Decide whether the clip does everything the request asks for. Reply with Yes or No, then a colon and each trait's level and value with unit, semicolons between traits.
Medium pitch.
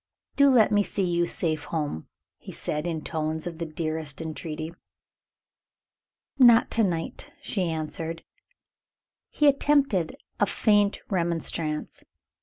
Yes: medium, 170 Hz